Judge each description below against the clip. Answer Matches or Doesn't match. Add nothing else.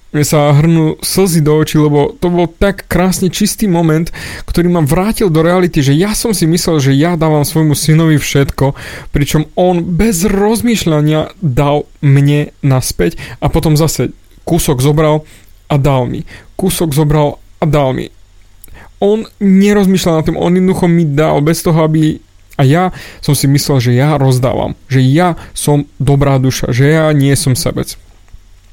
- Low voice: Doesn't match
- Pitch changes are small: Doesn't match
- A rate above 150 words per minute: Matches